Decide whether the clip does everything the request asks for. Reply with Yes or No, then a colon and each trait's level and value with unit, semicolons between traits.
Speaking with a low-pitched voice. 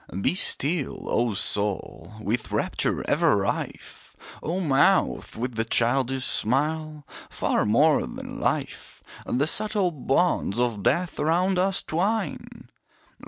No: medium, 145 Hz